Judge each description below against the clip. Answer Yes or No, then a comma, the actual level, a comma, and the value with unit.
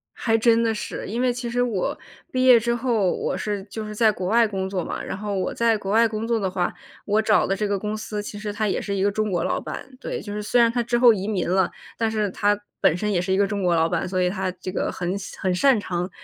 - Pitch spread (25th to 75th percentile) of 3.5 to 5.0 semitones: No, average, 3.0 semitones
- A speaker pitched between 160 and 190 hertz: No, high, 210 Hz